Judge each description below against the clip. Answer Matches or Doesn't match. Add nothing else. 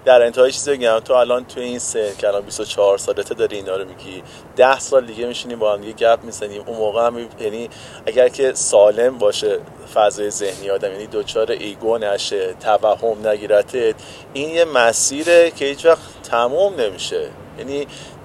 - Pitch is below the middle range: Doesn't match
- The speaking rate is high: Matches